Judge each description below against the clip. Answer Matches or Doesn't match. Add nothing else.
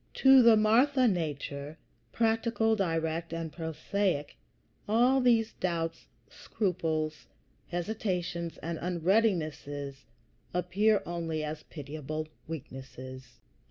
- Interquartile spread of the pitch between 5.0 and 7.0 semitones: Matches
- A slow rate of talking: Matches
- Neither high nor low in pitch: Matches